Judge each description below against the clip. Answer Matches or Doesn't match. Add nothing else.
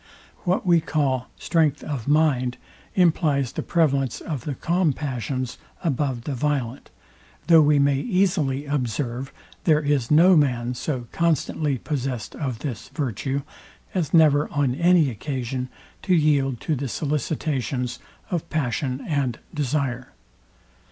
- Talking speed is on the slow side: Matches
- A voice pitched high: Doesn't match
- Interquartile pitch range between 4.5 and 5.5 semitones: Doesn't match